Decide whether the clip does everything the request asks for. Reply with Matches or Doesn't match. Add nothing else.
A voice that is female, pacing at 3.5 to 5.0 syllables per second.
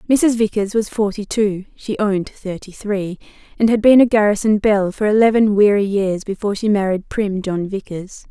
Matches